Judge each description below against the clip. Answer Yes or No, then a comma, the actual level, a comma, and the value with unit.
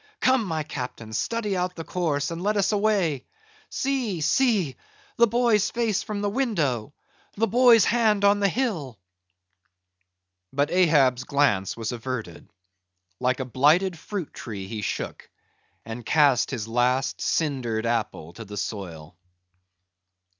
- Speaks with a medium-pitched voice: Yes, medium, 155 Hz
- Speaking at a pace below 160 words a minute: Yes, slow, 135 wpm